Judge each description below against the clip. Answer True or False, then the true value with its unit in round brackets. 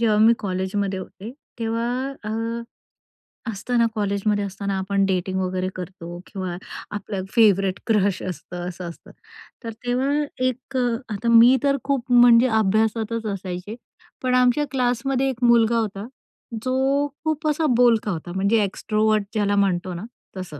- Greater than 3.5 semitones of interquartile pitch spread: True (4.2 semitones)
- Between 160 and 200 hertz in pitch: False (215 Hz)